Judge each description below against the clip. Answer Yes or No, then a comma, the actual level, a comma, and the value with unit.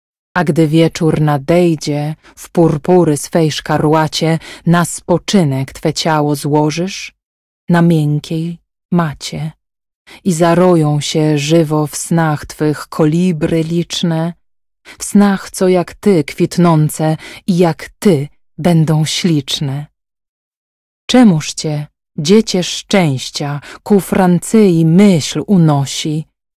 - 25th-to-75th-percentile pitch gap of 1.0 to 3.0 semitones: Yes, average, 2.7 semitones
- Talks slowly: Yes, slow, 100 wpm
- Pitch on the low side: No, medium, 165 Hz